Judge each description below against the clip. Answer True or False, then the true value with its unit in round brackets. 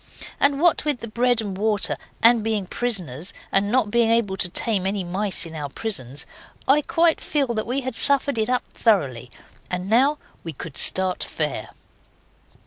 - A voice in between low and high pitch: False (215 Hz)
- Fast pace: False (175 wpm)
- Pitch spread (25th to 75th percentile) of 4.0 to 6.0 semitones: True (5.2 semitones)